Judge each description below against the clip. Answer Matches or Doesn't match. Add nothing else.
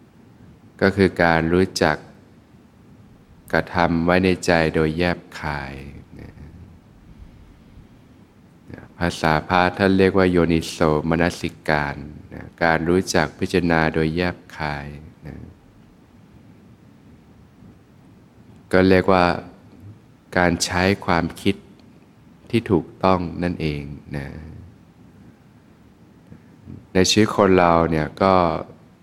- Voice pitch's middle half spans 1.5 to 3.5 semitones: Matches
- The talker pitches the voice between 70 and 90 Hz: Matches